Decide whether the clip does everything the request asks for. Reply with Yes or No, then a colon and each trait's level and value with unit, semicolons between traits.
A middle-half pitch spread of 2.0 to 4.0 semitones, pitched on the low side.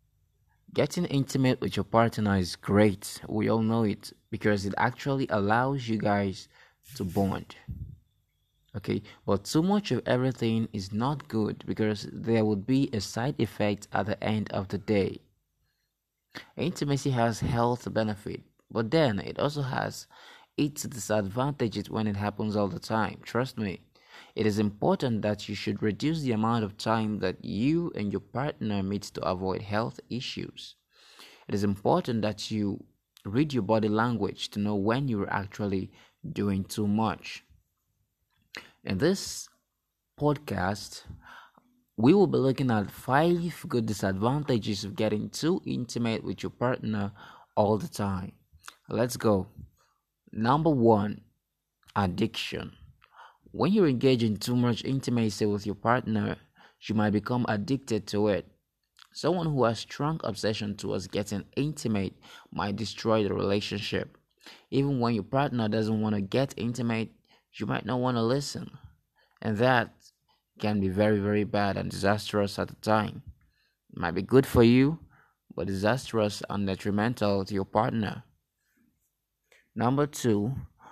Yes: average, 3.2 semitones; low, 110 Hz